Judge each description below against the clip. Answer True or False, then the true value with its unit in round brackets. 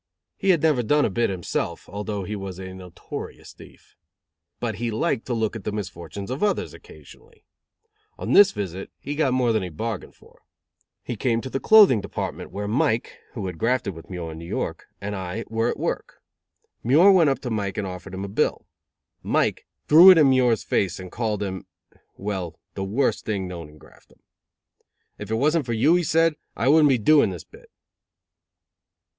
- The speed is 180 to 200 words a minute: True (195 wpm)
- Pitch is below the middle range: True (110 Hz)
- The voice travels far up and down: True (5.9 semitones)